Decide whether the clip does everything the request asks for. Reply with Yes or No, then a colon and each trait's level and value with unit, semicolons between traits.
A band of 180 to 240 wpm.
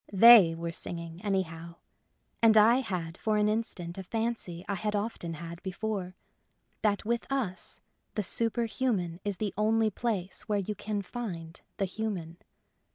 No: average, 150 wpm